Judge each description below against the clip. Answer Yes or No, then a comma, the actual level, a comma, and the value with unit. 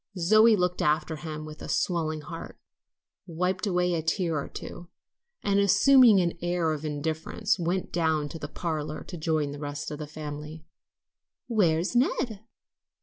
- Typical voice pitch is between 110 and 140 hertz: No, medium, 165 Hz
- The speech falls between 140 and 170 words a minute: Yes, average, 155 wpm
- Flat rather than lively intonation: No, average, 3.0 semitones